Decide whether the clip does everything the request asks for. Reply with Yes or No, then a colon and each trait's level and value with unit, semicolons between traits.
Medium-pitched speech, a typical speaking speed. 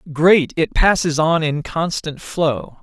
Yes: medium, 160 Hz; average, 150 wpm